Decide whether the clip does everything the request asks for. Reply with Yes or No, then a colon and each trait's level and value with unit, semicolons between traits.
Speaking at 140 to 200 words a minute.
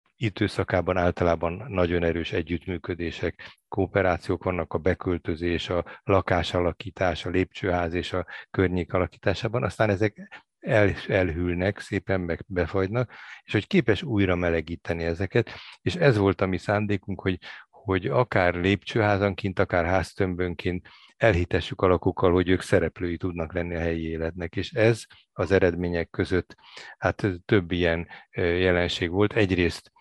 No: average, 130 wpm